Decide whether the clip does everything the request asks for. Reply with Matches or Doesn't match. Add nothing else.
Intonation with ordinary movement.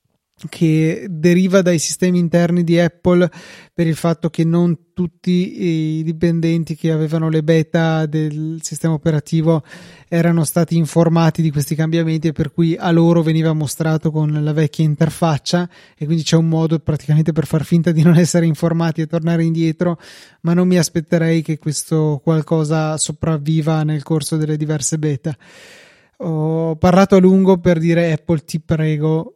Doesn't match